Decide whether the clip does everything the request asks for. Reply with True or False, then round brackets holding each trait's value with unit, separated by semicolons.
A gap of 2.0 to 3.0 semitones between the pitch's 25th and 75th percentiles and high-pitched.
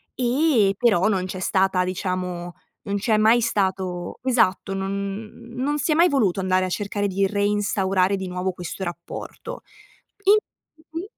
False (3.7 semitones; 195 Hz)